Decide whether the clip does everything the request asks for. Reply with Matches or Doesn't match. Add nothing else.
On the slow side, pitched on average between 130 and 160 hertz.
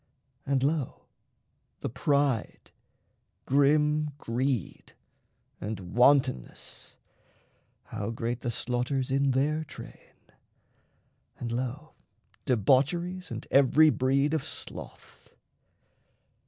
Matches